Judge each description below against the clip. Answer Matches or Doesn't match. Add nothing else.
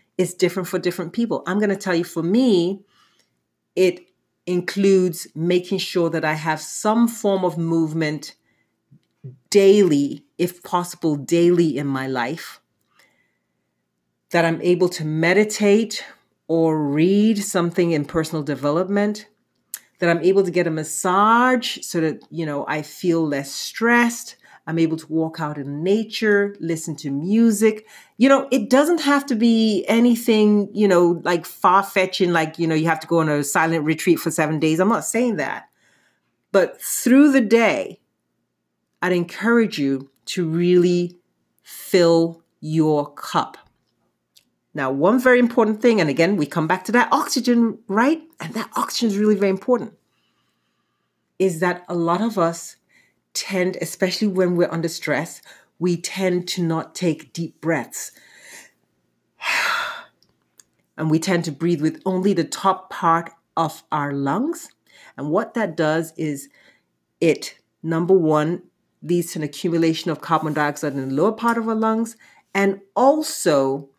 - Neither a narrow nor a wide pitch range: Matches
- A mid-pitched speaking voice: Matches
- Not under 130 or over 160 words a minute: Matches